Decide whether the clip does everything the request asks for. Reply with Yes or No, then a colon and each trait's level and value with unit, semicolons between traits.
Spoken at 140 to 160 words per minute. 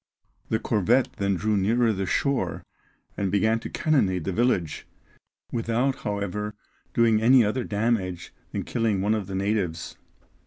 Yes: average, 150 wpm